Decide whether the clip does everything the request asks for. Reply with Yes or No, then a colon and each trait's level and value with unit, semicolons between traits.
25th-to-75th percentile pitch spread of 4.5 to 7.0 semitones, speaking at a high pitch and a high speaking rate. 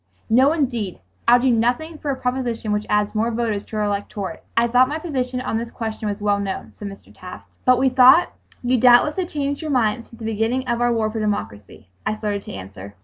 No: average, 3.5 semitones; high, 230 Hz; fast, 225 wpm